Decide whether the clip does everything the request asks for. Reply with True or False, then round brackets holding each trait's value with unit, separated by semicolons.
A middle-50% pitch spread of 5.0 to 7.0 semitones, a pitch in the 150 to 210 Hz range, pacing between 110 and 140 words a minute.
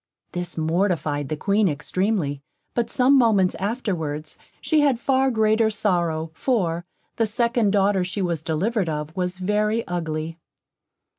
True (5.3 semitones; 190 Hz; 135 wpm)